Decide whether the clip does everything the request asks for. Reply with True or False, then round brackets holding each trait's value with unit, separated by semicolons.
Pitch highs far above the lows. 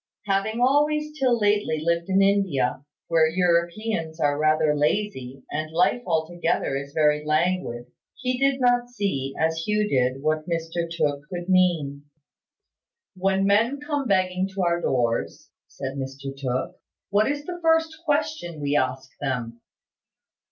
True (6.4 semitones)